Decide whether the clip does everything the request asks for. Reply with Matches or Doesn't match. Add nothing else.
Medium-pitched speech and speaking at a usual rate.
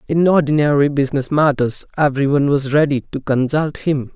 Matches